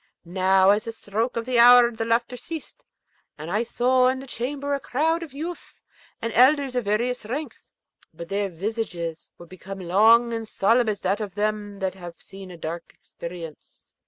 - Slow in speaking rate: No, average, 185 wpm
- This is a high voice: Yes, high, 220 Hz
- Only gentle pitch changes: No, average, 4.6 semitones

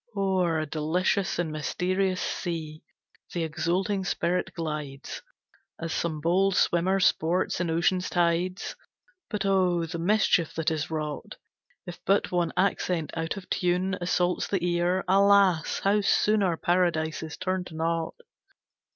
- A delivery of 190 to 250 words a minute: No, average, 140 wpm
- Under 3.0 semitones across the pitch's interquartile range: Yes, narrow, 2.4 semitones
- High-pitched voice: No, medium, 175 Hz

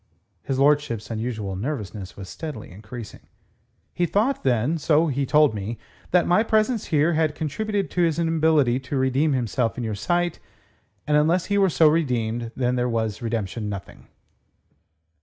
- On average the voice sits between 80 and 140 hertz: Yes, low, 135 Hz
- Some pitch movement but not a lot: No, wide, 6.2 semitones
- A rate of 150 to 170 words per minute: Yes, average, 155 wpm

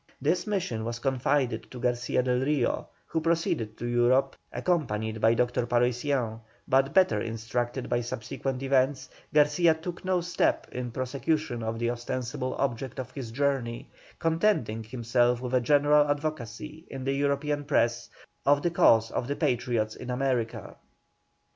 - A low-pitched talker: Yes, low, 130 Hz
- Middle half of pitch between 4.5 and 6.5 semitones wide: No, average, 3.5 semitones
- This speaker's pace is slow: No, average, 150 wpm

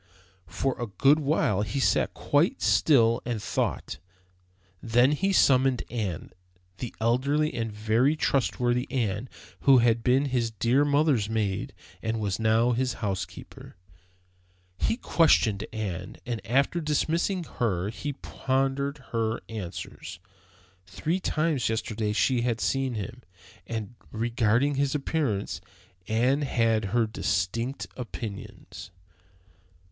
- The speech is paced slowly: Yes, slow, 120 wpm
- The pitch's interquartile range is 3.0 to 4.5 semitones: Yes, average, 3.8 semitones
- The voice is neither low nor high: No, low, 120 Hz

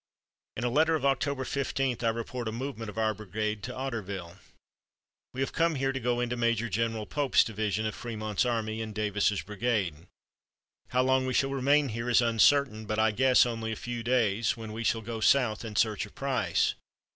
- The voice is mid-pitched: No, low, 115 Hz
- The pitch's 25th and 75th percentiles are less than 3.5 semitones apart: Yes, average, 3.1 semitones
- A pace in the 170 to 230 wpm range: Yes, average, 195 wpm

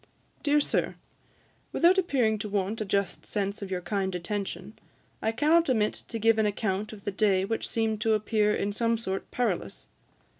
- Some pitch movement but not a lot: No, narrow, 2.3 semitones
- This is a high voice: Yes, high, 215 Hz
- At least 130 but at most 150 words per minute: No, average, 180 wpm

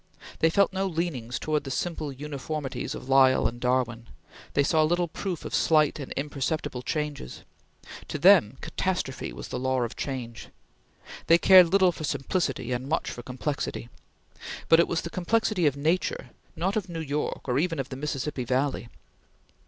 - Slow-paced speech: No, average, 170 wpm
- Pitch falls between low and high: Yes, medium, 150 Hz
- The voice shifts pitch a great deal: No, average, 4.4 semitones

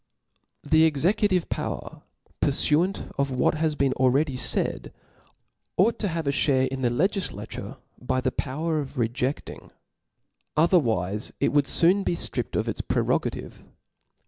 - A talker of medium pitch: Yes, medium, 145 Hz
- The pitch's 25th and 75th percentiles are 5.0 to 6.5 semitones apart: No, average, 4.4 semitones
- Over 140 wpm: No, slow, 135 wpm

